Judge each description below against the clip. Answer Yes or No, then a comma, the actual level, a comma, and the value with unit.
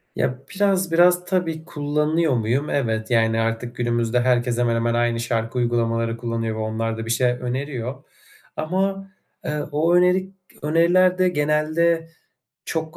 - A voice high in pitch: No, low, 130 Hz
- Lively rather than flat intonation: Yes, wide, 6.0 semitones